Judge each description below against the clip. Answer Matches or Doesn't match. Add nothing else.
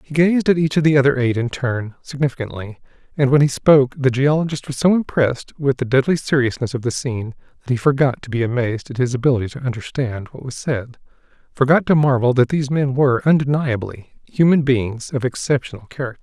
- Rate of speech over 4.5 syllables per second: Matches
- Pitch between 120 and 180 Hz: Matches